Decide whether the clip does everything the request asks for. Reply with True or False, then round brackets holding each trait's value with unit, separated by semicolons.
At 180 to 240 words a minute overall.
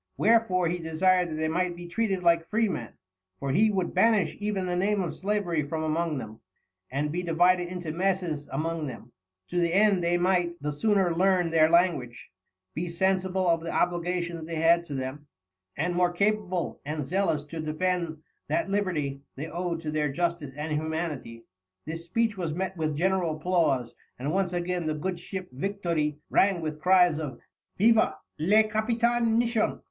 False (170 wpm)